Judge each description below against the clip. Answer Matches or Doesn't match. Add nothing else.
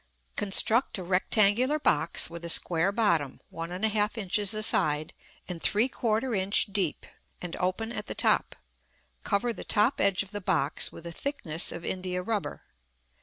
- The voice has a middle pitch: Doesn't match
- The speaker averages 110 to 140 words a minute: Doesn't match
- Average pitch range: Matches